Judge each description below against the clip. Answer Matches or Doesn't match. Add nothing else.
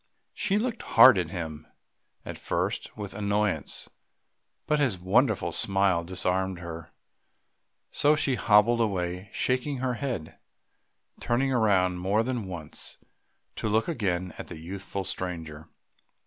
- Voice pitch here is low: Matches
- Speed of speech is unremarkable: Doesn't match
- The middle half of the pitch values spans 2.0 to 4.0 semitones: Doesn't match